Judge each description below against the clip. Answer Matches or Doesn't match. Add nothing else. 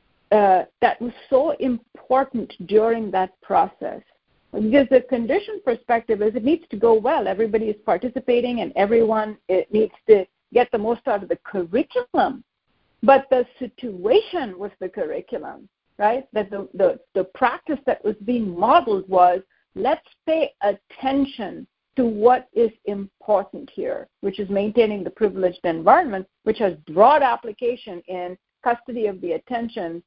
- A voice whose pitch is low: Doesn't match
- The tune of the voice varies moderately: Matches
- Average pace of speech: Matches